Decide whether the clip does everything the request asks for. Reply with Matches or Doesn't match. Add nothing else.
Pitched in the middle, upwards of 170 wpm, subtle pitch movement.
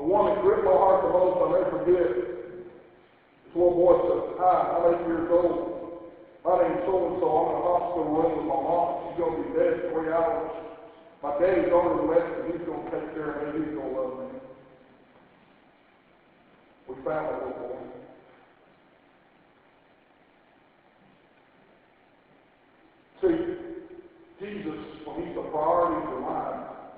Doesn't match